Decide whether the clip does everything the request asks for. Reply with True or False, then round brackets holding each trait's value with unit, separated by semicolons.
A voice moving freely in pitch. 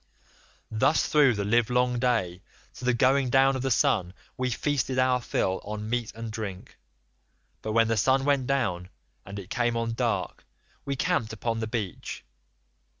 False (3.0 semitones)